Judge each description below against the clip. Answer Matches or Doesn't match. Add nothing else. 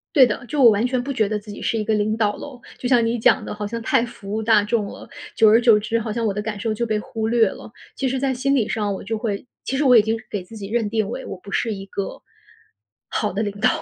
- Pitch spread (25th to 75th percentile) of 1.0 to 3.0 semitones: Matches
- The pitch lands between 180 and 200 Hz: Doesn't match